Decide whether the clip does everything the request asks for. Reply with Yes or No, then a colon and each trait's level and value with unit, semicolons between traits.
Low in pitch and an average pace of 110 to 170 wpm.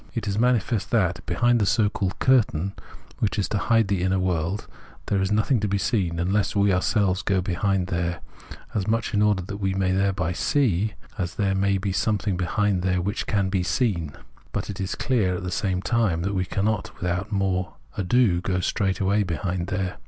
No: very low, 95 Hz; average, 200 wpm